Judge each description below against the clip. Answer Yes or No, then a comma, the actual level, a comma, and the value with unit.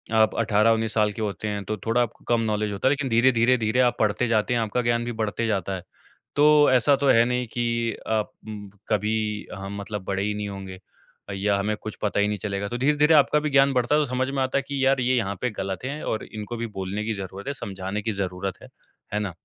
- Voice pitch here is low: Yes, low, 110 Hz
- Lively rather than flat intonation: No, average, 3.4 semitones